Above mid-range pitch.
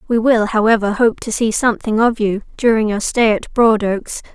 Yes: high, 220 Hz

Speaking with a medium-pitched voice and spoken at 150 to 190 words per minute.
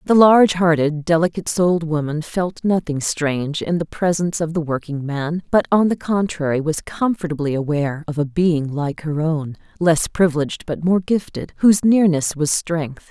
Yes: medium, 165 Hz; average, 170 wpm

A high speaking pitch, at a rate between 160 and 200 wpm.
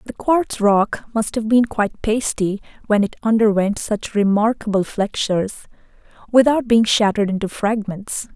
No: high, 215 Hz; slow, 135 wpm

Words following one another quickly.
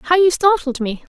Yes: fast, 210 wpm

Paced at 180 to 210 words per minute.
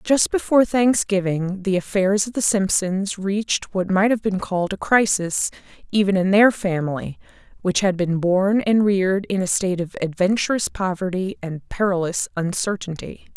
No: average, 155 wpm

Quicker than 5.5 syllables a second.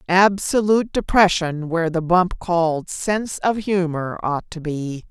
No: 4.3 syllables/s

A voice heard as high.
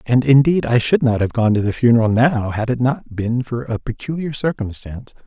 No: low, 120 Hz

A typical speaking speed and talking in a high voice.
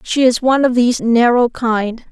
Yes: average, 170 wpm; high, 240 Hz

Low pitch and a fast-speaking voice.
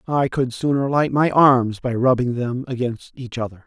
No: low, 130 Hz; average, 195 wpm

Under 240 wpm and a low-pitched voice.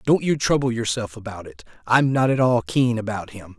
Yes: average, 200 wpm; low, 120 Hz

